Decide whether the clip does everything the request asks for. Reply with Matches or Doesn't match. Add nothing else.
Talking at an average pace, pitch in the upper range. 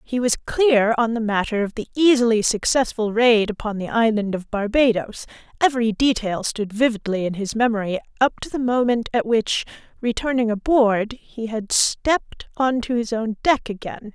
Matches